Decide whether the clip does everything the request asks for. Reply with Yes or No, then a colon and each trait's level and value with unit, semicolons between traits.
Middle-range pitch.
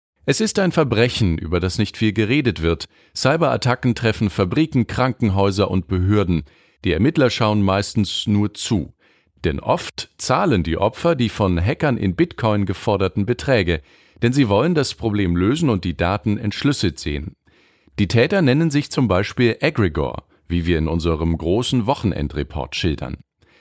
No: low, 105 Hz